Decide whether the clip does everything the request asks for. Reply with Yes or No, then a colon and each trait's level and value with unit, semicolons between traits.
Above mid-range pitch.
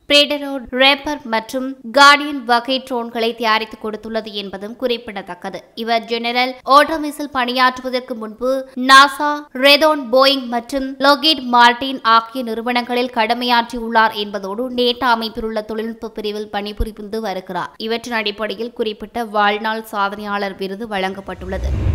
Yes: high, 235 Hz